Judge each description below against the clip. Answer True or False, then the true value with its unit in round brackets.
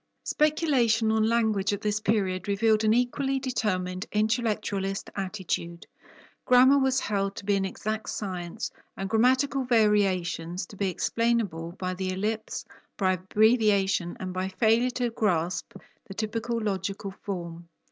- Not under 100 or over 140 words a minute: True (135 wpm)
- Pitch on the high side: True (210 Hz)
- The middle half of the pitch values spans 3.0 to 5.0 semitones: True (3.4 semitones)